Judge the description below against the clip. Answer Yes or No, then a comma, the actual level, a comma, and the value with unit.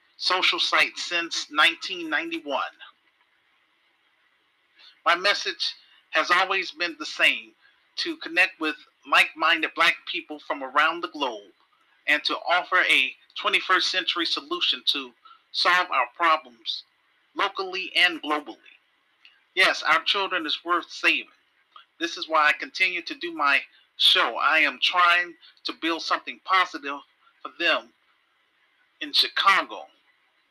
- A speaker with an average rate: No, slow, 120 wpm